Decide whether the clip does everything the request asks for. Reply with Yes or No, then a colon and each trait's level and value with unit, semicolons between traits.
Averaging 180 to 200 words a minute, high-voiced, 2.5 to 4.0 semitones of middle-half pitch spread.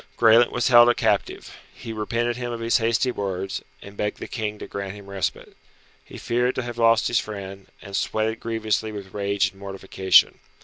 No: average, 190 wpm; low, 110 Hz; average, 2.9 semitones